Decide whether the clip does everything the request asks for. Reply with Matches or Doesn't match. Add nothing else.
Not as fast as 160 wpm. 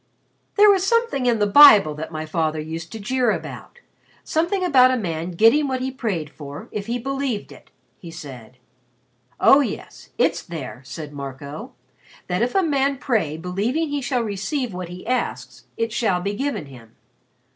Doesn't match